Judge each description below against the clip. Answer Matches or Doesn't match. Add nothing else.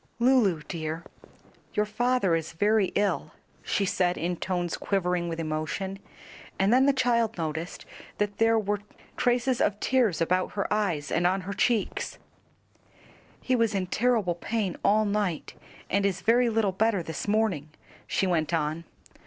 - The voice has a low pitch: Doesn't match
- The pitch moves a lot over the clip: Doesn't match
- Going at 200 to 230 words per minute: Doesn't match